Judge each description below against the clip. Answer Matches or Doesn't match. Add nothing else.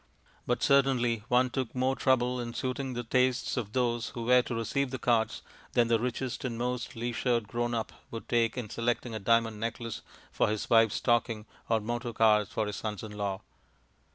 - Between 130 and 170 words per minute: Doesn't match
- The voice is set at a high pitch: Doesn't match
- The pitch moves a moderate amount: Doesn't match